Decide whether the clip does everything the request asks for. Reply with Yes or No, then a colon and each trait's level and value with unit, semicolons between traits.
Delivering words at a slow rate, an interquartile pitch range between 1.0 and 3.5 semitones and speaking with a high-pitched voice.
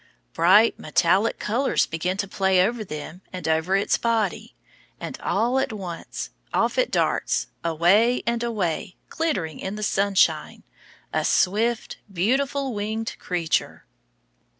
No: slow, 125 wpm; average, 4.4 semitones; high, 200 Hz